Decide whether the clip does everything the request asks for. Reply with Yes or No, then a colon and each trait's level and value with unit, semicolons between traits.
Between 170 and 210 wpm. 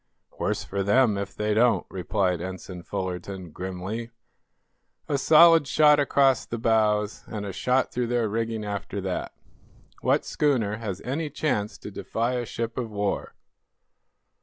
No: average, 145 wpm